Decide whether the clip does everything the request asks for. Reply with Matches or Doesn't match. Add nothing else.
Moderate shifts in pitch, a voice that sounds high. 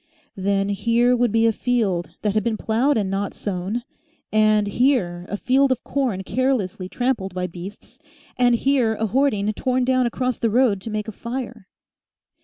Matches